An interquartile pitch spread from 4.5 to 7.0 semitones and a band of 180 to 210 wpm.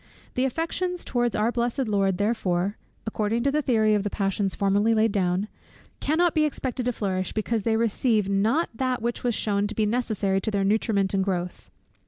No: average, 3.4 semitones; average, 190 wpm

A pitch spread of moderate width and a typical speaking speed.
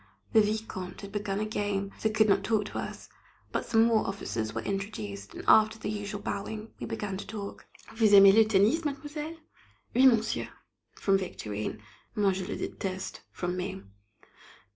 No: narrow, 2.3 semitones; average, 170 wpm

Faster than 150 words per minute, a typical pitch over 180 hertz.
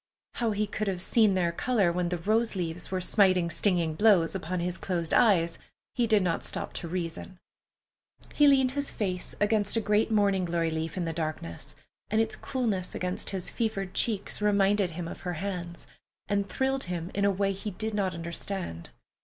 Yes: average, 185 wpm; high, 190 Hz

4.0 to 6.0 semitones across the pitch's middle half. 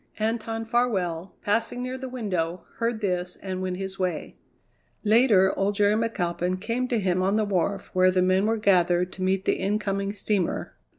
No: average, 3.2 semitones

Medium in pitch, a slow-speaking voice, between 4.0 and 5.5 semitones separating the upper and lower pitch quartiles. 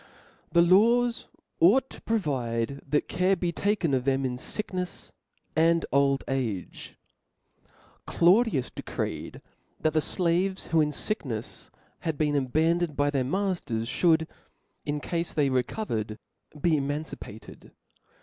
Yes: medium, 155 Hz; slow, 130 wpm; average, 5.1 semitones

